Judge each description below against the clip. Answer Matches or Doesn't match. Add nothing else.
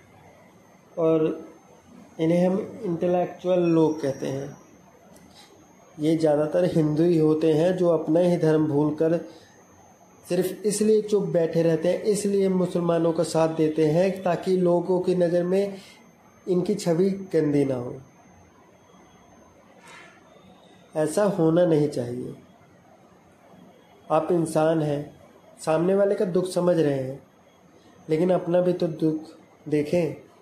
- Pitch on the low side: Doesn't match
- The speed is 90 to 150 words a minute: Matches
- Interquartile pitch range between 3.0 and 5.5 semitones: Doesn't match